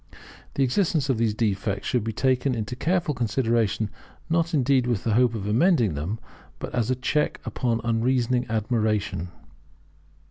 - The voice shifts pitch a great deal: No, average, 3.1 semitones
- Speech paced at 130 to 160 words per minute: Yes, average, 150 wpm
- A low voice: Yes, low, 120 Hz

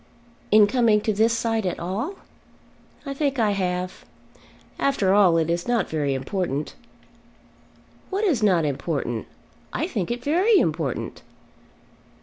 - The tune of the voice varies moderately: No, wide, 6.0 semitones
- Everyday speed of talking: No, slow, 130 wpm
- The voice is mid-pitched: No, high, 205 Hz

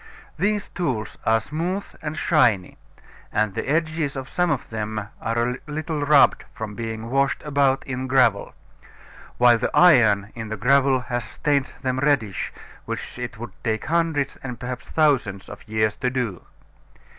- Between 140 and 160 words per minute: Yes, average, 155 wpm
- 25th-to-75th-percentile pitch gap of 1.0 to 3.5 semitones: No, average, 4.8 semitones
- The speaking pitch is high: No, low, 125 Hz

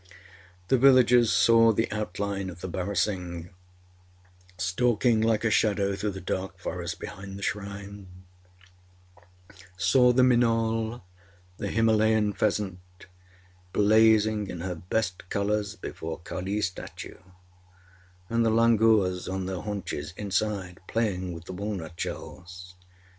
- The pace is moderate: No, slow, 115 wpm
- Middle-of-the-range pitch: No, low, 100 Hz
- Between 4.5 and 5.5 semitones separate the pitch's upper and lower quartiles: No, average, 3.3 semitones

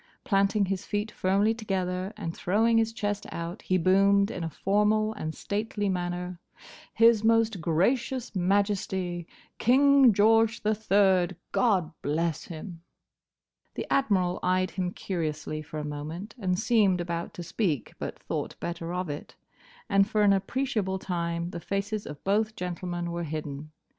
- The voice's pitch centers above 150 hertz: Yes, high, 190 Hz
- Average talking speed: Yes, average, 150 wpm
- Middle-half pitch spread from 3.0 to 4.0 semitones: Yes, average, 3.6 semitones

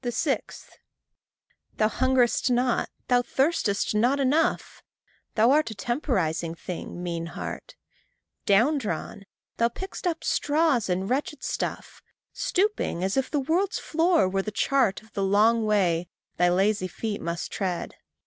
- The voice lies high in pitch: Yes, high, 230 Hz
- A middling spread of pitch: No, wide, 6.2 semitones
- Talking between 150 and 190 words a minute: No, average, 140 wpm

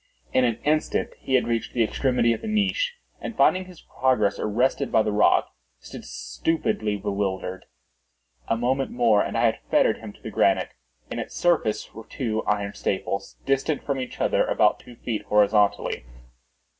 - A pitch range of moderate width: Yes, average, 4.5 semitones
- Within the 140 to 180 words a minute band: Yes, average, 170 wpm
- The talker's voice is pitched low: Yes, low, 120 Hz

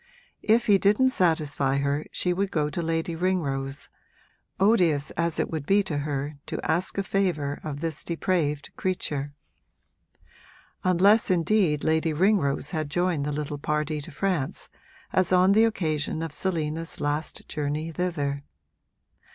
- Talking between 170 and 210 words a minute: No, average, 145 wpm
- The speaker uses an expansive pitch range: No, average, 4.0 semitones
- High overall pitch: No, medium, 160 Hz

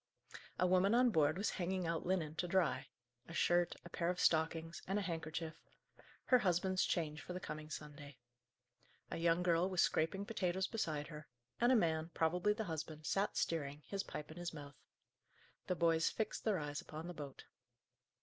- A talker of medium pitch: Yes, medium, 170 Hz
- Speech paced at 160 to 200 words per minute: Yes, average, 180 wpm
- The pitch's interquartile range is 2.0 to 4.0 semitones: Yes, average, 3.0 semitones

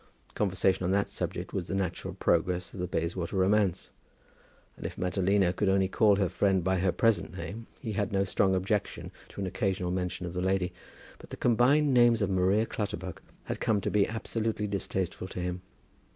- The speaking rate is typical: Yes, average, 190 wpm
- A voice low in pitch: Yes, very low, 95 Hz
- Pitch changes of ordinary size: No, narrow, 2.3 semitones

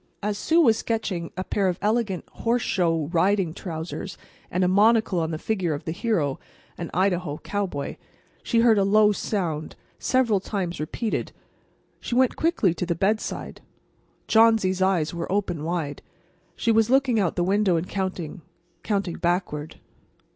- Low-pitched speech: No, high, 190 Hz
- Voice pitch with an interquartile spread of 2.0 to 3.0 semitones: No, average, 4.2 semitones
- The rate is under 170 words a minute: Yes, average, 150 wpm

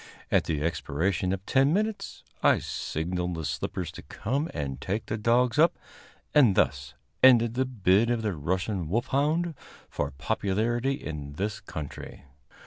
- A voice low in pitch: Yes, low, 100 Hz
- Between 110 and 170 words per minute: Yes, average, 145 wpm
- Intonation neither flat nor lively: No, wide, 7.4 semitones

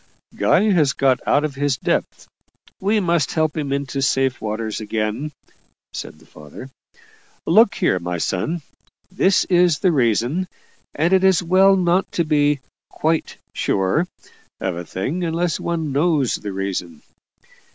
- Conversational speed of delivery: Yes, average, 145 wpm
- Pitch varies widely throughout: Yes, wide, 6.8 semitones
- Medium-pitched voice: Yes, medium, 145 Hz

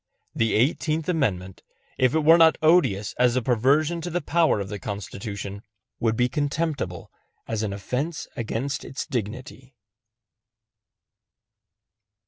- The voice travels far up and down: Yes, wide, 6.8 semitones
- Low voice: Yes, low, 125 Hz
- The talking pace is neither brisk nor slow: No, slow, 125 wpm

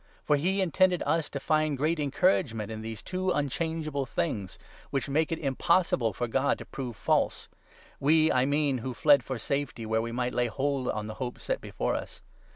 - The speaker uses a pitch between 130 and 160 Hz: Yes, medium, 140 Hz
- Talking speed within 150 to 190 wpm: No, average, 200 wpm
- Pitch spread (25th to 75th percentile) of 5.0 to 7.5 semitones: No, average, 4.5 semitones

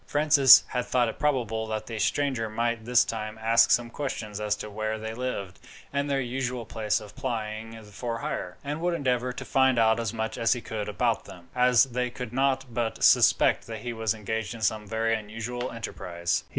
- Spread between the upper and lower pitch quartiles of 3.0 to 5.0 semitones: No, narrow, 2.5 semitones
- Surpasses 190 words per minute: Yes, average, 200 wpm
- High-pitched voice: No, low, 115 Hz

